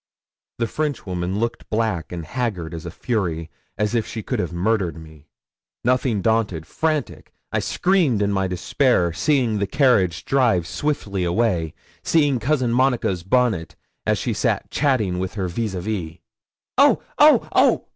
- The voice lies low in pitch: Yes, low, 105 Hz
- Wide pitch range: Yes, wide, 6.0 semitones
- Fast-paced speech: No, average, 155 wpm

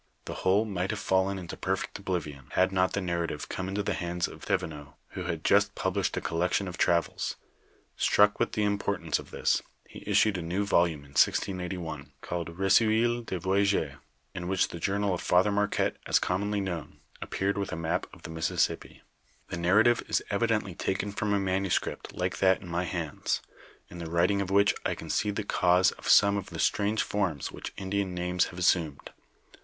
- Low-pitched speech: Yes, very low, 95 Hz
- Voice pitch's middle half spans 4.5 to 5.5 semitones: No, narrow, 2.6 semitones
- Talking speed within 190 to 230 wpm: Yes, average, 195 wpm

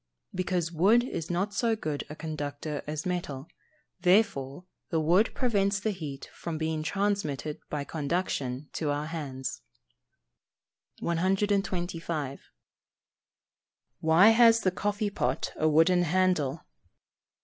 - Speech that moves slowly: Yes, slow, 115 wpm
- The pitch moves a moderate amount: Yes, average, 4.6 semitones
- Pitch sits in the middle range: Yes, medium, 165 Hz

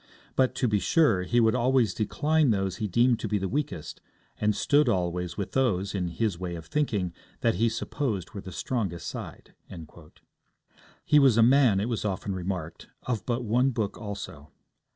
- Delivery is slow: No, average, 180 wpm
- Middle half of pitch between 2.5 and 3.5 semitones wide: No, average, 5.0 semitones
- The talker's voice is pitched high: No, low, 105 Hz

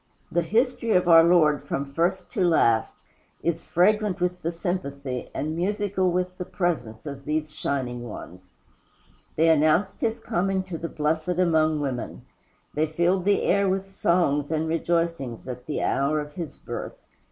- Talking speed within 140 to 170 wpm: Yes, average, 160 wpm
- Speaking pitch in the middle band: Yes, medium, 165 Hz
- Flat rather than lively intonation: No, average, 3.7 semitones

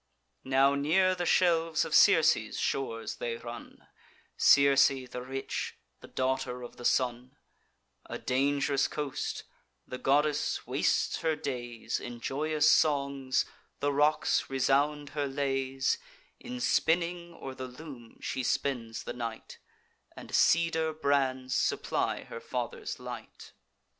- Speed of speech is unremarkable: No, slow, 125 wpm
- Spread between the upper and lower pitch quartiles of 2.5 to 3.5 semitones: Yes, average, 2.8 semitones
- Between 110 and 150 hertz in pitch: Yes, low, 135 Hz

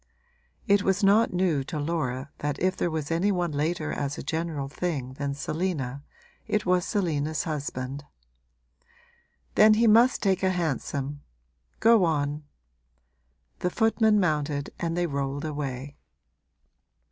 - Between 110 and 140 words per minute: Yes, slow, 135 wpm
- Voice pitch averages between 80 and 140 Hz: No, medium, 160 Hz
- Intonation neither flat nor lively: Yes, average, 4.6 semitones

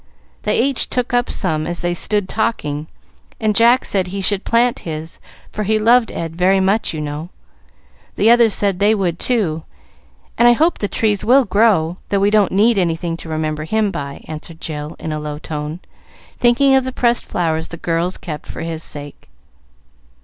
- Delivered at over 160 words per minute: Yes, average, 185 wpm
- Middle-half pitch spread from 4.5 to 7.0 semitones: Yes, wide, 5.6 semitones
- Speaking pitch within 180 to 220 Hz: Yes, high, 190 Hz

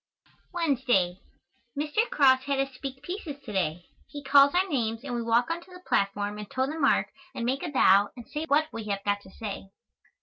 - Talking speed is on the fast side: Yes, fast, 210 wpm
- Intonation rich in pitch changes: Yes, wide, 6.0 semitones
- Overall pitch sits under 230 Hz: No, very high, 260 Hz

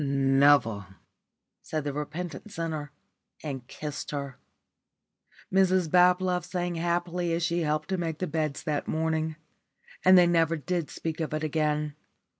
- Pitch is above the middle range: No, medium, 160 Hz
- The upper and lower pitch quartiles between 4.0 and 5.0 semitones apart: No, average, 2.8 semitones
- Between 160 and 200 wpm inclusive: No, average, 140 wpm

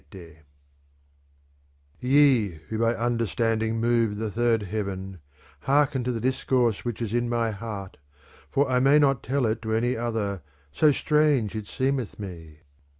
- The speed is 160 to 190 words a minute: No, average, 150 wpm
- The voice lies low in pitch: Yes, low, 115 Hz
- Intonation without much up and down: No, average, 3.2 semitones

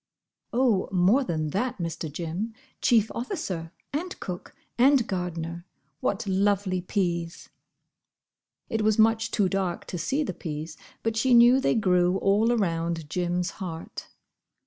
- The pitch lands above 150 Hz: Yes, high, 190 Hz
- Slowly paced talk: Yes, slow, 130 wpm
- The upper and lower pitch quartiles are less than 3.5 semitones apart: No, average, 4.8 semitones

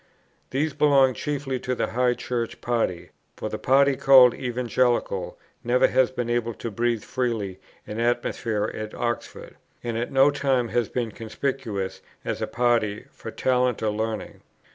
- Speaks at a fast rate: No, average, 160 wpm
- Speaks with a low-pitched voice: Yes, low, 120 Hz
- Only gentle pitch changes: Yes, narrow, 2.3 semitones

